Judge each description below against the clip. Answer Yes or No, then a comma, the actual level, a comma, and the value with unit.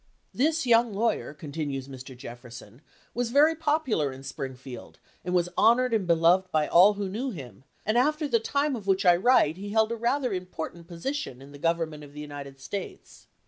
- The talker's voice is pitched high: No, medium, 180 Hz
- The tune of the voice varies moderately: No, wide, 8.5 semitones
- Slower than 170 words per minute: No, average, 185 wpm